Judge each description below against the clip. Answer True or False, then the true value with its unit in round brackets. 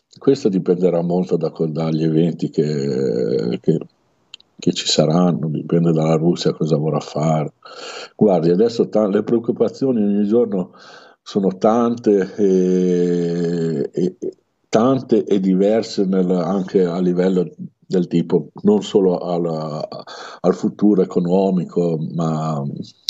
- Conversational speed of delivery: False (100 wpm)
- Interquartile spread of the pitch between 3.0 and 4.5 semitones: True (3.4 semitones)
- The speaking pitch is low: True (90 Hz)